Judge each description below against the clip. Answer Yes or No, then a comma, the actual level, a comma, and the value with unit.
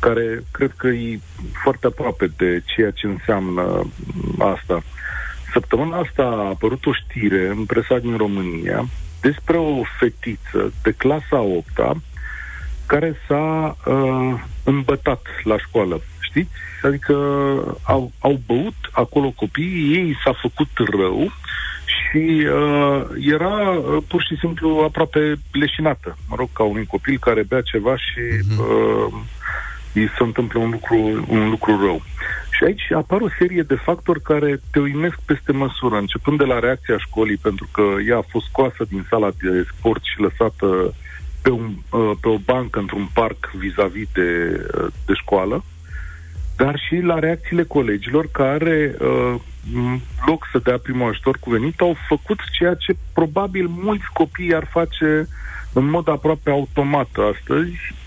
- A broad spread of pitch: Yes, wide, 6.6 semitones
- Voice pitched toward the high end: No, low, 125 Hz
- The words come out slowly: No, average, 145 wpm